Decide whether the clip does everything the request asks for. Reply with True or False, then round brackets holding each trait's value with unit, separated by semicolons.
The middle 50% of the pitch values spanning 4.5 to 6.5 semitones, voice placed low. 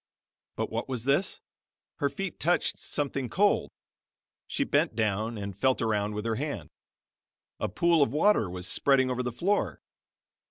True (5.3 semitones; 130 Hz)